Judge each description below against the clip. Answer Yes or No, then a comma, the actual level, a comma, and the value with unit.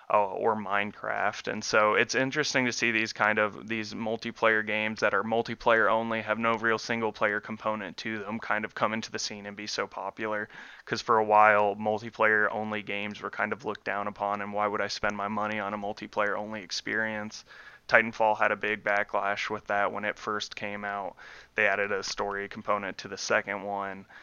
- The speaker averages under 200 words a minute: No, fast, 205 wpm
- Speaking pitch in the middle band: No, low, 105 Hz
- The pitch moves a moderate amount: No, narrow, 1.3 semitones